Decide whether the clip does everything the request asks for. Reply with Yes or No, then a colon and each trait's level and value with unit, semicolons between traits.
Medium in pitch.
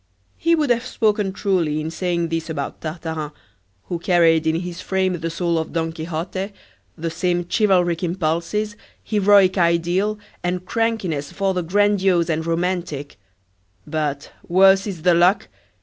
Yes: medium, 175 Hz